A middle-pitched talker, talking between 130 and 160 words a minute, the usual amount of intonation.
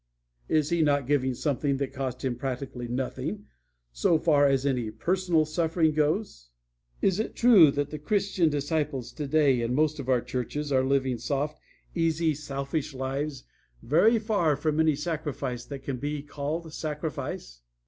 Yes: medium, 145 Hz; average, 155 wpm; average, 3.1 semitones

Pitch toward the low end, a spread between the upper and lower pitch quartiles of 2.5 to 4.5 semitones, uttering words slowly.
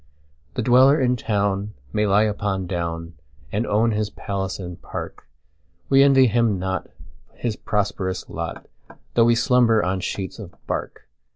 Yes: low, 100 Hz; average, 4.0 semitones; slow, 130 wpm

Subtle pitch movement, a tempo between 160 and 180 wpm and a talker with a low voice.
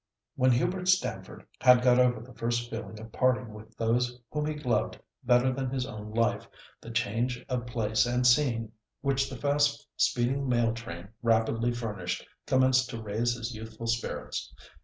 Yes: narrow, 2.1 semitones; average, 165 wpm; low, 120 Hz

